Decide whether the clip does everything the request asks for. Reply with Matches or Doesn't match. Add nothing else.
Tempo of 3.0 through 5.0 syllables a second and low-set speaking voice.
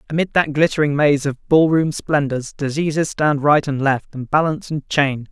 Doesn't match